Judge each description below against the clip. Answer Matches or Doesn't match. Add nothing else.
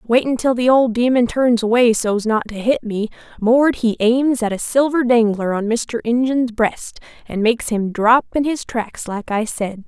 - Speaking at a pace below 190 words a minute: Doesn't match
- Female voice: Matches